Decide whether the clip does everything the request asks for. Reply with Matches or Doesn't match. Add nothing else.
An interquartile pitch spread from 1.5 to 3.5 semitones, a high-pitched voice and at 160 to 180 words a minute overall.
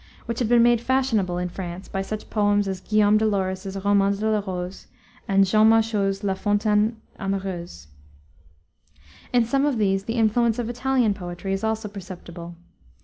Matches